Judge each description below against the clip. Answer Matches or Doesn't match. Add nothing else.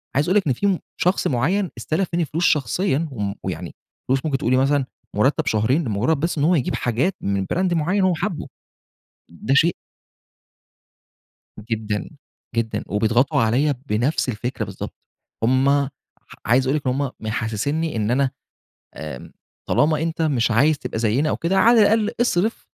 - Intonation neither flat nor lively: Doesn't match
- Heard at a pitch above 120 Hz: Matches